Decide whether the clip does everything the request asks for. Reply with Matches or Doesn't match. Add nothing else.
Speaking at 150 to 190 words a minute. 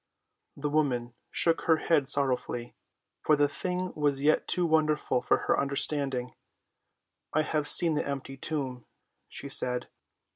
Doesn't match